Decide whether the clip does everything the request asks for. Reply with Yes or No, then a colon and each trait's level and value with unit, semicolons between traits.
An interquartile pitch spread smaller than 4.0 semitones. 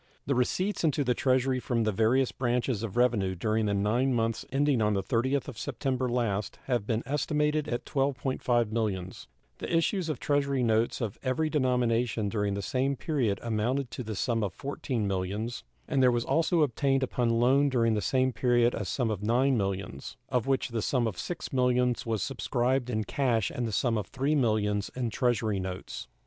Yes: average, 3.5 semitones